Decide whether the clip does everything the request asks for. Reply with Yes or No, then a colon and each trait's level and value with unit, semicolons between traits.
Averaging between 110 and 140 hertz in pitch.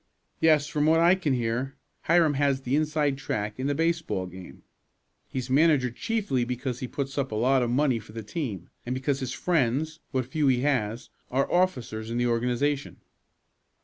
Yes: low, 135 Hz